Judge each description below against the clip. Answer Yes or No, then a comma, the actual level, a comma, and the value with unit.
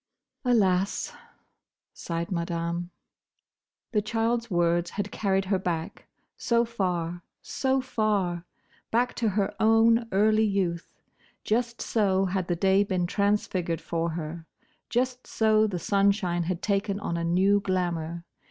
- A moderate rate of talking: No, slow, 125 wpm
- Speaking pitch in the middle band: No, high, 195 Hz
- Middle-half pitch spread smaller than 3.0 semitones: No, average, 3.9 semitones